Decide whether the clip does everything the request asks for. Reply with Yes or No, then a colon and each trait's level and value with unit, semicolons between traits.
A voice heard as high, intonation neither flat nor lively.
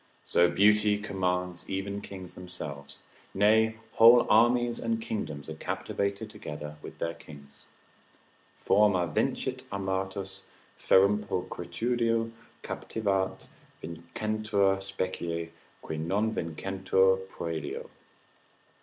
No: very low, 95 Hz; average, 3.6 semitones